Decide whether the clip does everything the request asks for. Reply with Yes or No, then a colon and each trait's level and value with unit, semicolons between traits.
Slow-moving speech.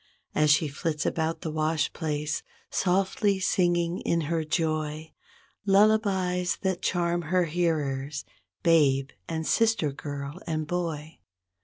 Yes: slow, 120 wpm